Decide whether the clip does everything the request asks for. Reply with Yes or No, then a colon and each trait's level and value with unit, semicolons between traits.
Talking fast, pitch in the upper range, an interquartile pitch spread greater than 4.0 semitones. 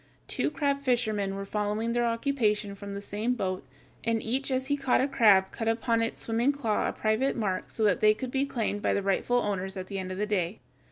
No: fast, 230 wpm; high, 220 Hz; average, 3.5 semitones